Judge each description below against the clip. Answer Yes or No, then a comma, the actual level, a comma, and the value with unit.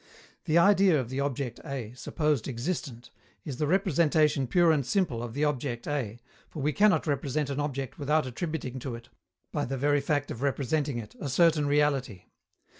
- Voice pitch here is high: No, medium, 145 Hz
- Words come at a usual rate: Yes, average, 180 wpm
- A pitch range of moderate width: Yes, average, 3.2 semitones